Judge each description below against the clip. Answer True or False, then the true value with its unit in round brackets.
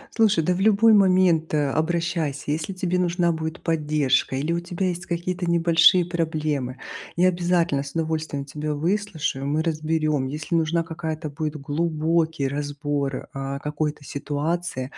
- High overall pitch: False (160 Hz)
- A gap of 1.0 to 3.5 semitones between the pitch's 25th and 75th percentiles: True (2.7 semitones)